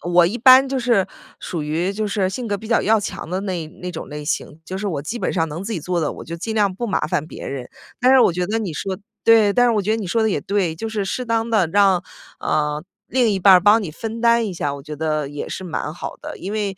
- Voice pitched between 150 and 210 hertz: Yes, high, 195 Hz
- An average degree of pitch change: Yes, average, 5.0 semitones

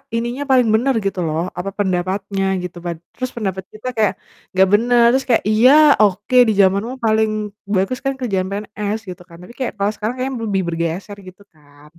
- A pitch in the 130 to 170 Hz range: No, high, 205 Hz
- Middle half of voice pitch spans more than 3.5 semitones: Yes, average, 4.1 semitones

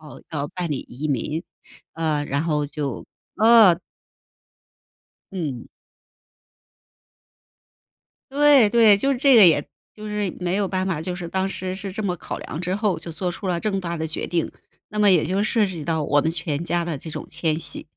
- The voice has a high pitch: No, medium, 175 Hz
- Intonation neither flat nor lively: Yes, average, 4.4 semitones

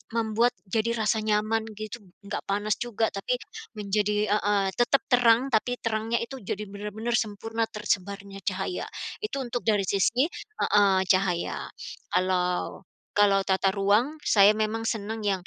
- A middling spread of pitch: No, narrow, 2.3 semitones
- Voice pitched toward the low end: No, high, 210 Hz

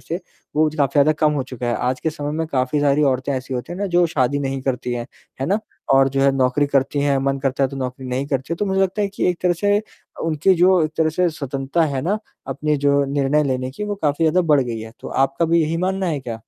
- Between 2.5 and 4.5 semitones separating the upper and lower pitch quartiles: Yes, average, 3.7 semitones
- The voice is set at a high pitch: No, medium, 145 Hz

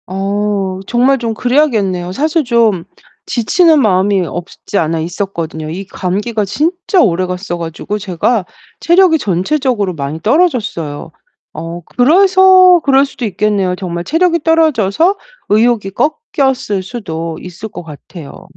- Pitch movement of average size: No, wide, 7.2 semitones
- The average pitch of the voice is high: Yes, high, 205 Hz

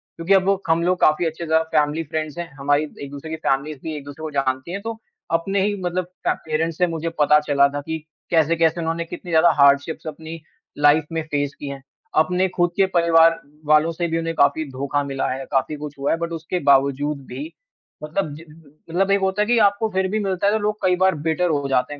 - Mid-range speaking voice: Yes, medium, 160 Hz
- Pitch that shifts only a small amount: No, average, 3.3 semitones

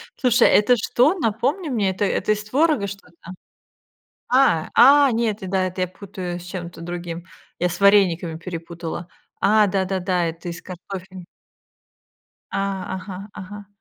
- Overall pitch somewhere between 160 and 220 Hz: Yes, high, 190 Hz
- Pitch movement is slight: No, average, 3.2 semitones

